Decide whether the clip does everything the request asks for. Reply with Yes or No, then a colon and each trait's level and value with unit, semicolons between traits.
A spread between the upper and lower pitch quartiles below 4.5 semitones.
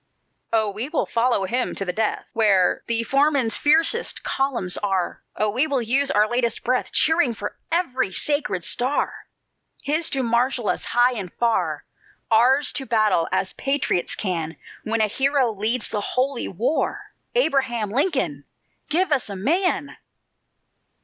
No: average, 4.8 semitones